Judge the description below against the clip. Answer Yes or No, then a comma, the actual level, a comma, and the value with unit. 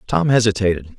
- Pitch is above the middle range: No, low, 105 Hz